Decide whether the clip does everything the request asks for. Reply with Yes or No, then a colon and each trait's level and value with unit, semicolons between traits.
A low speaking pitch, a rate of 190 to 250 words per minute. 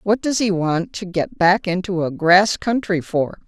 No: medium, 185 Hz; fast, 205 wpm